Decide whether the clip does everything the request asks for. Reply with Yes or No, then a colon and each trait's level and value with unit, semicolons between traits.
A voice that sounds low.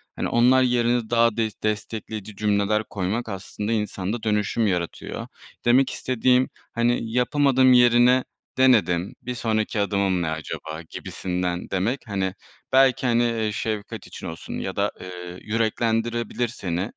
Yes: low, 110 Hz